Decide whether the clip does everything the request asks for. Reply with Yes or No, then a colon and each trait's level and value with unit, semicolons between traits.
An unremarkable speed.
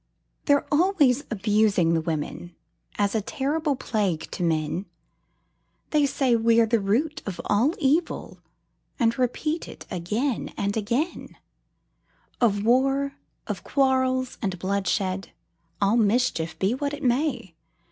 No: slow, 125 wpm